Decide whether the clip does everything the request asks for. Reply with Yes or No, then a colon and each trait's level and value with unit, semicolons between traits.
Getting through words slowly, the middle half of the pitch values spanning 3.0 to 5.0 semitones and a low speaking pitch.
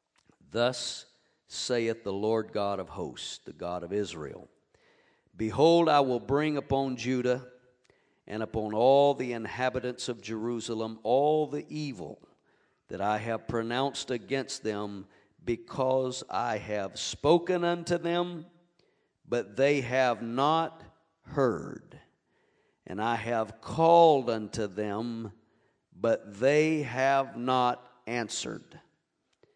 Yes: slow, 110 wpm; average, 3.8 semitones; low, 125 Hz